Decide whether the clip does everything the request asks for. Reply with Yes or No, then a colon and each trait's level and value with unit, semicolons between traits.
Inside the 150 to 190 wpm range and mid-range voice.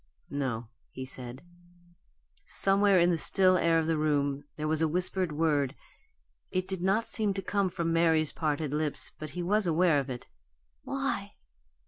Yes: average, 165 wpm; medium, 165 Hz